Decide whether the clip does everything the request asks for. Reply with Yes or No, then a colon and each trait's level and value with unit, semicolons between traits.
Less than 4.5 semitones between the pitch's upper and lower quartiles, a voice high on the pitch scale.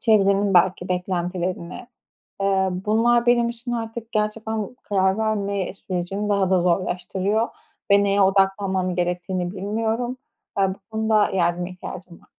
Yes: average, 3.0 semitones; high, 195 Hz